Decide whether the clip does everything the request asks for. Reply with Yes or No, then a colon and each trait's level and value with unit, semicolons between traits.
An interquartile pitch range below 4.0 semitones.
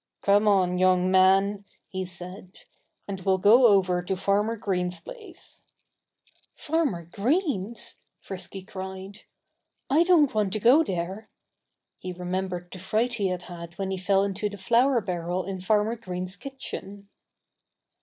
Yes: average, 2.8 semitones